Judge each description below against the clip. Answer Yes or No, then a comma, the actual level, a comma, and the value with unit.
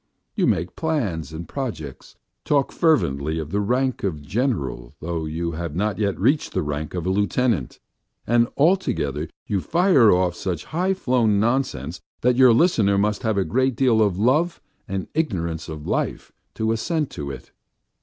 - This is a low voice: Yes, low, 100 Hz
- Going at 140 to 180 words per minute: Yes, average, 165 wpm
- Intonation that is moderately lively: No, wide, 7.9 semitones